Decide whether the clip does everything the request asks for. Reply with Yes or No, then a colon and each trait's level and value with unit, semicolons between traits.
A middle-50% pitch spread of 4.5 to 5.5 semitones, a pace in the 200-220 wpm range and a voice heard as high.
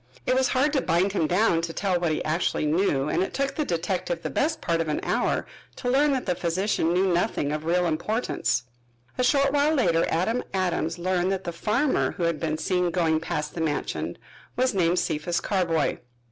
No: average, 5.2 semitones; fast, 205 wpm; medium, 180 Hz